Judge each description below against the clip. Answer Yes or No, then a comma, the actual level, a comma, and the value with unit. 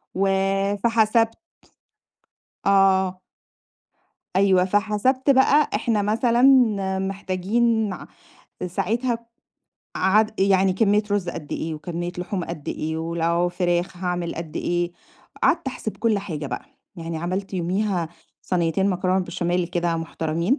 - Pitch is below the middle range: No, high, 190 Hz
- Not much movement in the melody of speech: No, average, 3.3 semitones